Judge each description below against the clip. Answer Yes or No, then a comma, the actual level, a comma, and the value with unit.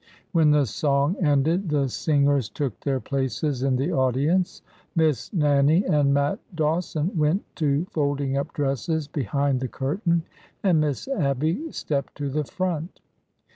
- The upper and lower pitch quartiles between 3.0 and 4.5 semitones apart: No, narrow, 2.6 semitones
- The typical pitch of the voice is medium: Yes, medium, 145 Hz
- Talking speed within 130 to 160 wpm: Yes, average, 140 wpm